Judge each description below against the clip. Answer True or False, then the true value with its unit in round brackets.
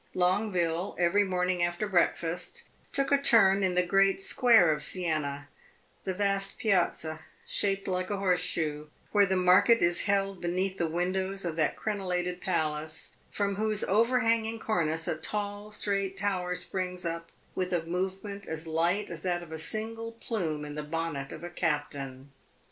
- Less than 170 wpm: True (160 wpm)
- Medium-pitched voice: True (180 Hz)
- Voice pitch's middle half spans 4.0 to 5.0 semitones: False (3.3 semitones)